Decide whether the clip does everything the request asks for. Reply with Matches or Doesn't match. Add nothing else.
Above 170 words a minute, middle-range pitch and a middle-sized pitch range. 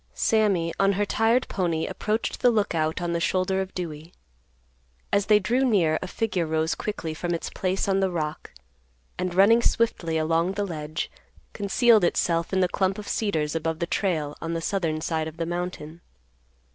Matches